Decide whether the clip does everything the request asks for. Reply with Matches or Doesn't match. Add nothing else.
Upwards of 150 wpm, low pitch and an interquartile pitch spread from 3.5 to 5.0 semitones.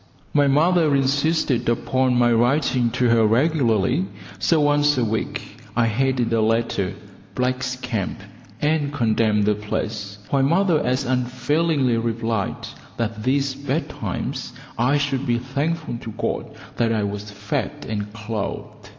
Doesn't match